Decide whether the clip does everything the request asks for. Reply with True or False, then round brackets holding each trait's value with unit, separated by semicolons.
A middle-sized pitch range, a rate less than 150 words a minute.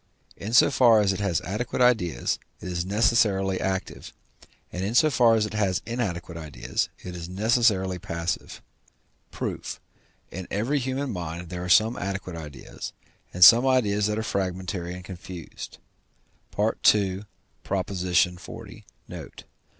True (3.9 semitones; 140 wpm)